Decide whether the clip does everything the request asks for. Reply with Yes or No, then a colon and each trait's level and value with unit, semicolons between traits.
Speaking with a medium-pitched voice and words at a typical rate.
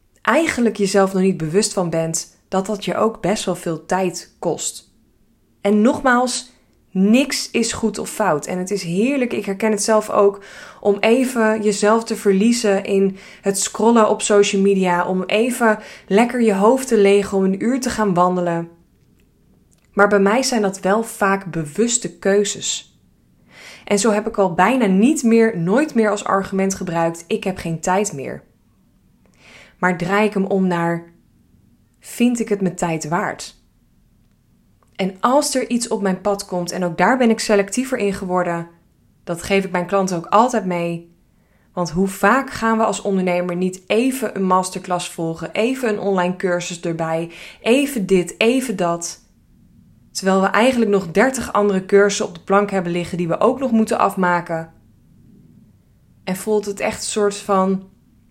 No: high, 200 Hz; average, 170 wpm